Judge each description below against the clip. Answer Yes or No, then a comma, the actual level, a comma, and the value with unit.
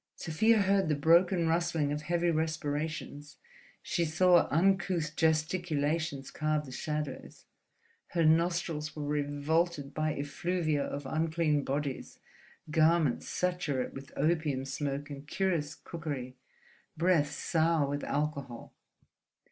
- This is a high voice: No, medium, 155 Hz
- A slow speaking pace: Yes, slow, 110 wpm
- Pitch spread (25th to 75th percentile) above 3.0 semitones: No, average, 2.7 semitones